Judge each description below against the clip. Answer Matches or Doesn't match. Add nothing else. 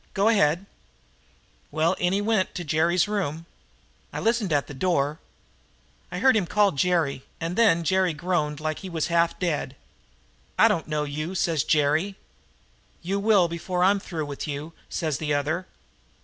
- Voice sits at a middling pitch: Matches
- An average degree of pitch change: Matches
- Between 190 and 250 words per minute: Doesn't match